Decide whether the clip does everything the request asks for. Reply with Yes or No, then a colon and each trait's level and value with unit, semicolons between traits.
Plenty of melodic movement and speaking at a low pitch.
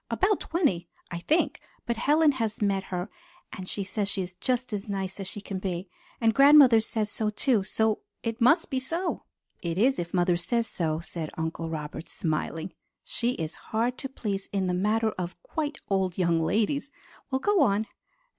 No: wide, 5.8 semitones; high, 205 Hz